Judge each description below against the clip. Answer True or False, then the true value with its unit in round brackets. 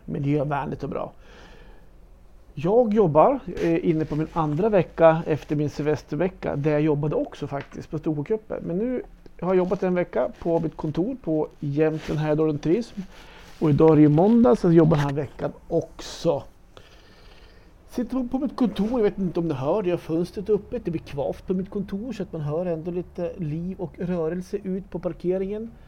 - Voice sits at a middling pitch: True (170 Hz)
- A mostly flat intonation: False (4.0 semitones)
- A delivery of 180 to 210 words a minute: True (190 wpm)